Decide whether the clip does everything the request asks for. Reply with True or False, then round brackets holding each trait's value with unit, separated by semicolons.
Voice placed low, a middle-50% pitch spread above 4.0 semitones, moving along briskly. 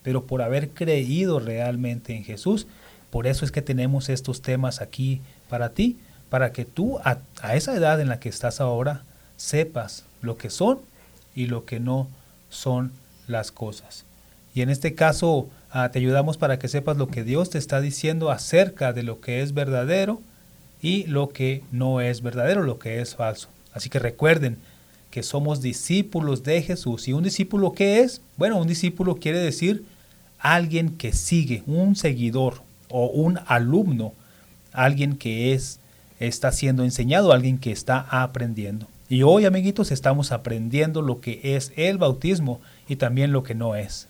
False (130 Hz; 4.5 semitones; 170 wpm)